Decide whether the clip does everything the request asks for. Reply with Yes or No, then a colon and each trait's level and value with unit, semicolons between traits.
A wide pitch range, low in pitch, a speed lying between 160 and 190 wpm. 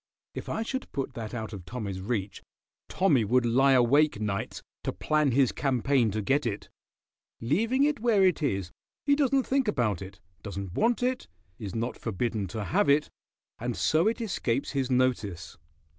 Yes: wide, 8.6 semitones; low, 125 Hz; average, 175 wpm